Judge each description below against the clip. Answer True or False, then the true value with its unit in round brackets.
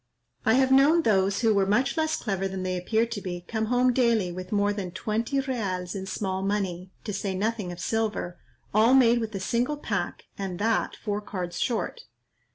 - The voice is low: False (210 Hz)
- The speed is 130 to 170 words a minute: False (195 wpm)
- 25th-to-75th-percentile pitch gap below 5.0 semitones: True (3.6 semitones)